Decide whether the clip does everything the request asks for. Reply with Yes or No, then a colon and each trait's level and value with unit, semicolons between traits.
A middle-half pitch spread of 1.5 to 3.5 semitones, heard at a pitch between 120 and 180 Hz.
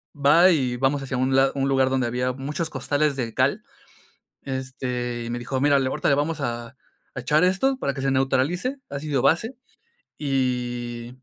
Yes: narrow, 2.6 semitones; low, 135 Hz